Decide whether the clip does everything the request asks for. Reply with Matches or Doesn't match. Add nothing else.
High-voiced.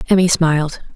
Doesn't match